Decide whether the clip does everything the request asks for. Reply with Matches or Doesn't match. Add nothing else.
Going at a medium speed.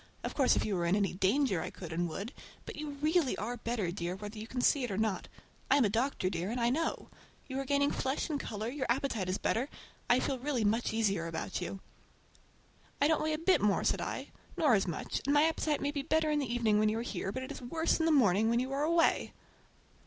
Doesn't match